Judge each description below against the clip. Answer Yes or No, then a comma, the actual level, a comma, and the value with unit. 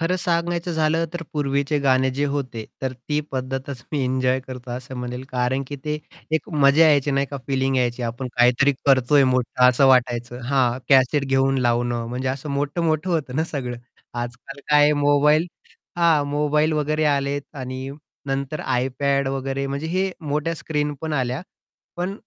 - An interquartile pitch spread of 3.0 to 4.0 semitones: No, narrow, 2.6 semitones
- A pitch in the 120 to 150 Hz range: Yes, medium, 140 Hz